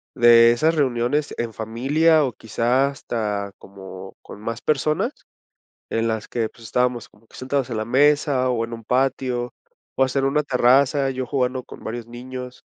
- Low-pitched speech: Yes, low, 125 Hz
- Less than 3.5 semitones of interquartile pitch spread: Yes, average, 2.8 semitones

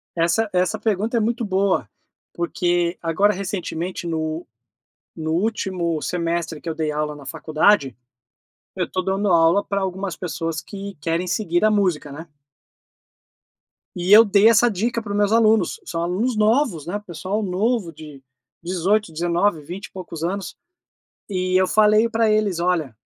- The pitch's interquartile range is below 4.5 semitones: Yes, average, 3.8 semitones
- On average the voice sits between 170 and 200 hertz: Yes, medium, 185 Hz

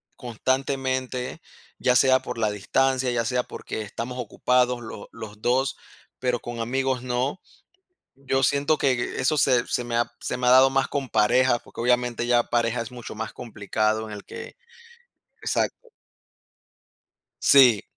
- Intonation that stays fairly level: Yes, narrow, 2.0 semitones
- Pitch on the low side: Yes, low, 125 Hz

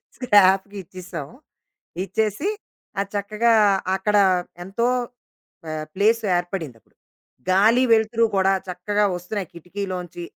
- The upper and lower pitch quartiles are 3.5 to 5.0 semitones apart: No, average, 3.0 semitones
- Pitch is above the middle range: Yes, high, 200 Hz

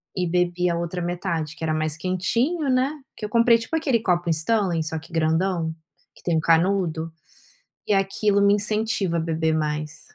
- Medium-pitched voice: Yes, medium, 175 Hz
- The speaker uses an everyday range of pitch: Yes, average, 4.3 semitones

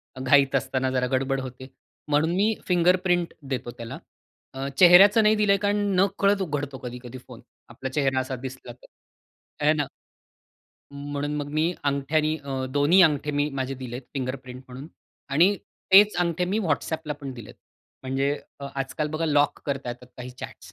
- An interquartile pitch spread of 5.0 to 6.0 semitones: No, average, 4.5 semitones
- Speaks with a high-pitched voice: No, medium, 145 Hz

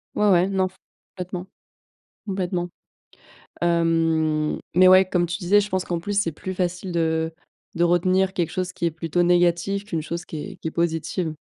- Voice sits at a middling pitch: Yes, medium, 175 Hz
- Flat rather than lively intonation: Yes, narrow, 2.1 semitones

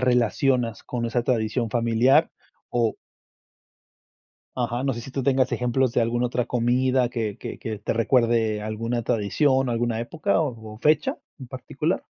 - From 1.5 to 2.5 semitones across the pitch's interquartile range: Yes, narrow, 2.1 semitones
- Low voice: Yes, low, 120 Hz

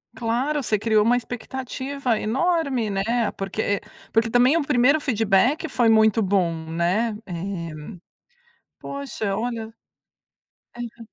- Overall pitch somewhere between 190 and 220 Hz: No, high, 230 Hz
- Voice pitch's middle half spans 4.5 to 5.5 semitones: No, average, 3.4 semitones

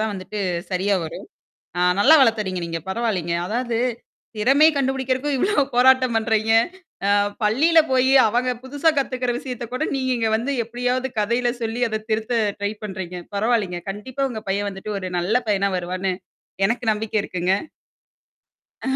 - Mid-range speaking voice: No, high, 225 Hz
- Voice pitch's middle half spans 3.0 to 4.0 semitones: No, average, 4.4 semitones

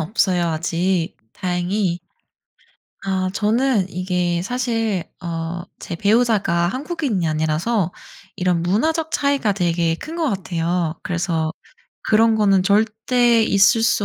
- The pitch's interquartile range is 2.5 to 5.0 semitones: Yes, average, 4.6 semitones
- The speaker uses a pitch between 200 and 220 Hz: No, high, 190 Hz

